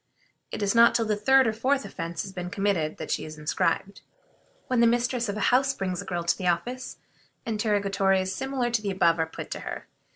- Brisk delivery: Yes, fast, 220 wpm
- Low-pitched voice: No, high, 205 Hz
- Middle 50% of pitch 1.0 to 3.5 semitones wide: No, average, 4.7 semitones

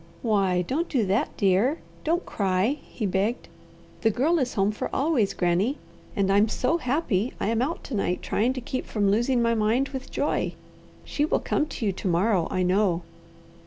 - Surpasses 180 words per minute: Yes, average, 190 wpm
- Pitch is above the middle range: Yes, high, 220 Hz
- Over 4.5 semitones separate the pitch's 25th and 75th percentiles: Yes, average, 5.1 semitones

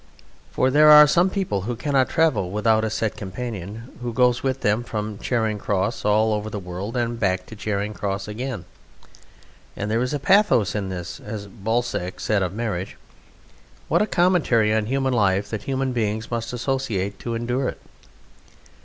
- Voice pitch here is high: No, low, 110 Hz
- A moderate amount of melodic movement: Yes, average, 3.6 semitones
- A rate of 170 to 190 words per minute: Yes, average, 175 wpm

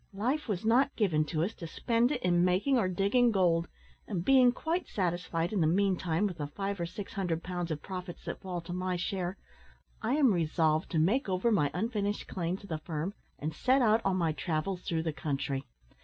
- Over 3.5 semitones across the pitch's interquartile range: Yes, average, 4.2 semitones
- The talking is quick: Yes, fast, 210 wpm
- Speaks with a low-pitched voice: No, medium, 185 Hz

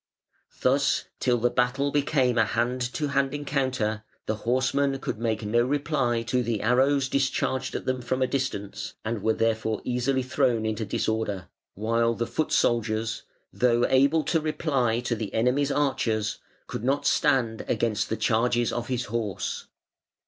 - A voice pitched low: Yes, low, 120 Hz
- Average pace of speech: Yes, average, 155 wpm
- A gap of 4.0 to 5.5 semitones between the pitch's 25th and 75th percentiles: No, average, 3.1 semitones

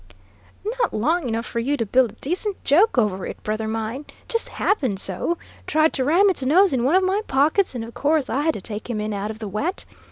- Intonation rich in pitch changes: Yes, wide, 7.8 semitones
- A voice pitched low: No, very high, 270 Hz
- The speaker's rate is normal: No, fast, 235 wpm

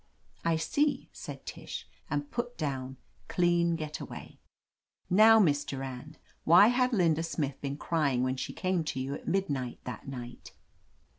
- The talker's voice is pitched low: No, medium, 155 Hz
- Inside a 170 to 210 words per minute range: No, average, 150 wpm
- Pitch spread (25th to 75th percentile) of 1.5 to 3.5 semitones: No, average, 5.0 semitones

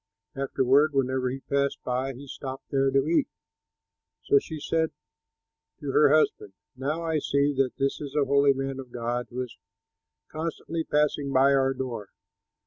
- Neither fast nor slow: Yes, average, 160 wpm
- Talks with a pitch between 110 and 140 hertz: Yes, low, 135 Hz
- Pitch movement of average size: No, narrow, 1.9 semitones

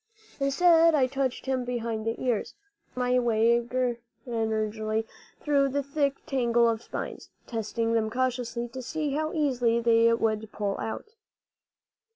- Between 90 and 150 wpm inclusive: Yes, average, 140 wpm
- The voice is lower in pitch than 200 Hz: No, high, 240 Hz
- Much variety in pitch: No, average, 3.0 semitones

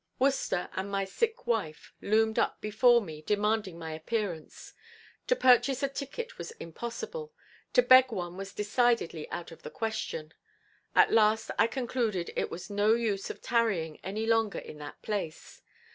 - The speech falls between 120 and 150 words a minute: No, average, 160 wpm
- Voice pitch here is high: Yes, high, 215 Hz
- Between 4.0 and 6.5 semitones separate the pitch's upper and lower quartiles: Yes, average, 4.8 semitones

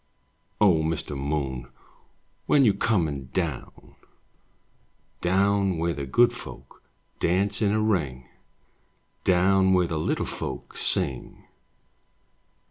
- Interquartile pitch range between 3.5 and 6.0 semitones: Yes, wide, 5.6 semitones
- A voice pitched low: Yes, very low, 90 Hz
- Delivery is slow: Yes, slow, 105 wpm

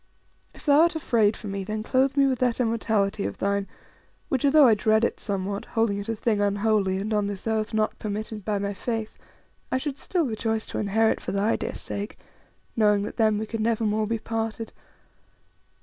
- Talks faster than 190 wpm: Yes, average, 200 wpm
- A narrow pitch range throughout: Yes, narrow, 2.0 semitones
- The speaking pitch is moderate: No, high, 220 Hz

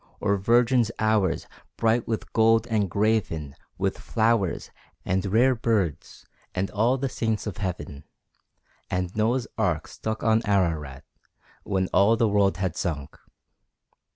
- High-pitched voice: No, low, 105 Hz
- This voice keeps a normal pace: No, slow, 130 wpm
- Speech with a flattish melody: No, average, 3.4 semitones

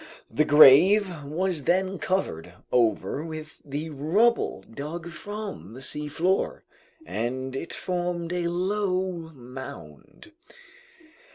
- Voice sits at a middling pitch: Yes, medium, 160 Hz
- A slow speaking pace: Yes, slow, 100 wpm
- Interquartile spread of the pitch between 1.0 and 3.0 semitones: No, average, 5.1 semitones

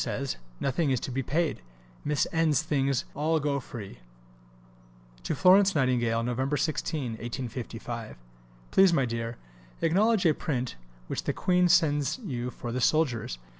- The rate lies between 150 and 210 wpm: No, average, 140 wpm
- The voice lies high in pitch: No, medium, 140 Hz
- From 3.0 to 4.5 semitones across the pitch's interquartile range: No, average, 5.1 semitones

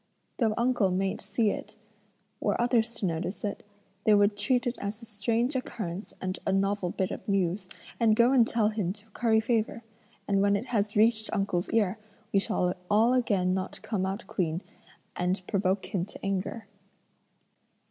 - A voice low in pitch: No, high, 205 Hz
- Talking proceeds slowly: No, average, 175 wpm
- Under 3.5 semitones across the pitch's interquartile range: Yes, average, 3.0 semitones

